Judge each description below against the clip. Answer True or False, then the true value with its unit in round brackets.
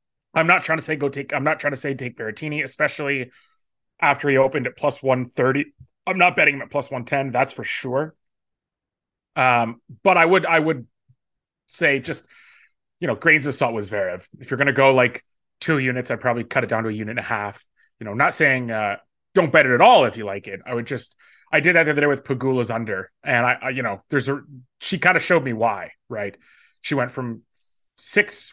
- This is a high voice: False (135 Hz)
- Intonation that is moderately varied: True (3.4 semitones)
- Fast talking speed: True (235 wpm)